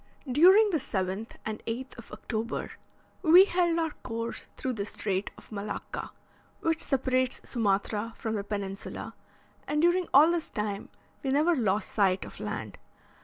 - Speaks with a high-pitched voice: Yes, high, 235 Hz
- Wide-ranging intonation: Yes, wide, 7.4 semitones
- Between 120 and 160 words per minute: Yes, average, 150 wpm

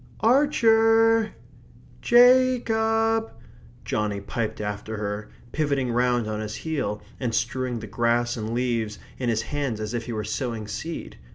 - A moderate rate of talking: Yes, average, 150 wpm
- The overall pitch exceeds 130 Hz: No, low, 120 Hz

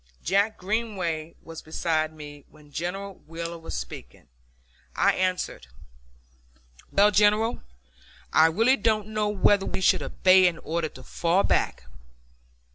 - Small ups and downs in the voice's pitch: No, average, 4.5 semitones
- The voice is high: No, medium, 180 Hz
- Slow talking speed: Yes, slow, 125 wpm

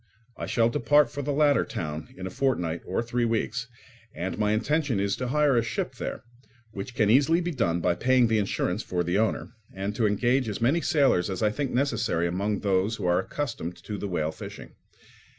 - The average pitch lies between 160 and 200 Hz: No, low, 110 Hz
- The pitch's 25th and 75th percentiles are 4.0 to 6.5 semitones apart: Yes, wide, 5.6 semitones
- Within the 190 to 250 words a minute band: Yes, fast, 205 wpm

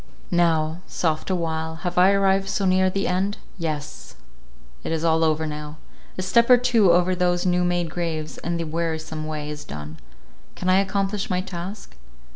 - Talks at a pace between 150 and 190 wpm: Yes, average, 160 wpm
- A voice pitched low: No, medium, 175 Hz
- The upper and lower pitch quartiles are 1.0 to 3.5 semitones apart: Yes, average, 2.9 semitones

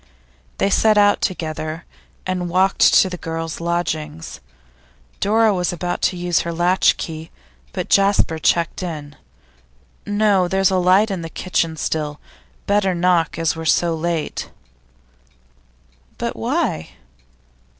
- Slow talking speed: Yes, slow, 130 wpm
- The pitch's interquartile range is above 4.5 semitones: No, narrow, 2.6 semitones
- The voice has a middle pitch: Yes, medium, 175 Hz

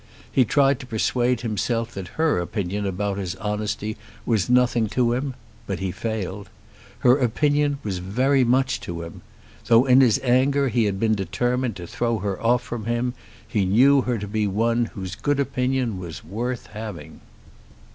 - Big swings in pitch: No, average, 4.0 semitones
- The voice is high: No, low, 115 Hz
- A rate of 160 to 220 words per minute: Yes, average, 165 wpm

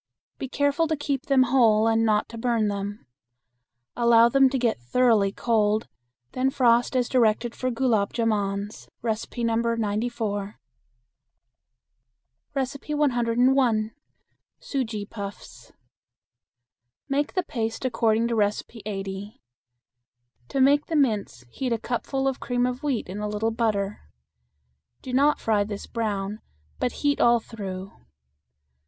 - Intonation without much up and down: No, average, 3.5 semitones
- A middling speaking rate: No, slow, 125 wpm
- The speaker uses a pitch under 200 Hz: No, high, 230 Hz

